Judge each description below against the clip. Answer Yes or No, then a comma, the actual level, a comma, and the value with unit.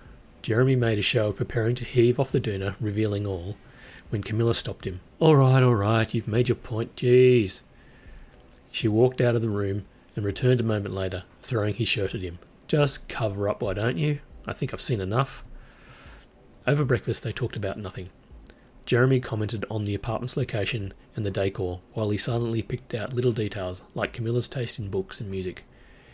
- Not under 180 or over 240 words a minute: Yes, average, 190 wpm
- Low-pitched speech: Yes, low, 115 Hz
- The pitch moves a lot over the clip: No, average, 3.5 semitones